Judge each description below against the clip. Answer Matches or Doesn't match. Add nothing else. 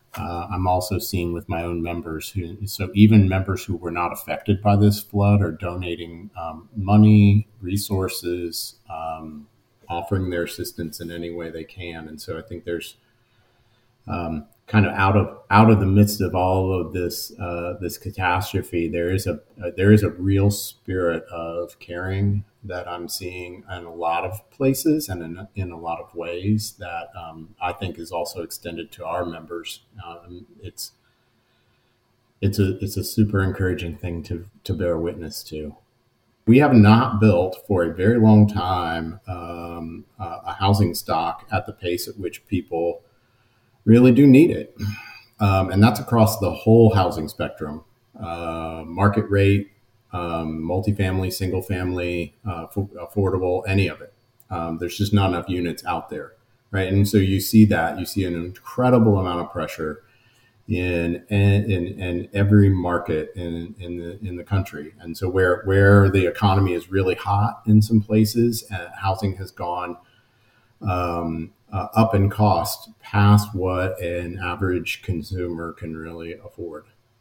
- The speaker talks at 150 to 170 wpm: Matches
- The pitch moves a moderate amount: Matches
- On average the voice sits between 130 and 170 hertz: Doesn't match